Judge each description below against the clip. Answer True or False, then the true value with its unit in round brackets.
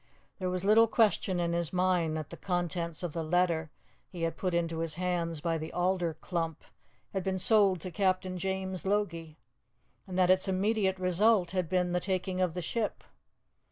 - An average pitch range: False (2.0 semitones)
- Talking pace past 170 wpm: True (185 wpm)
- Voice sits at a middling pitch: True (180 Hz)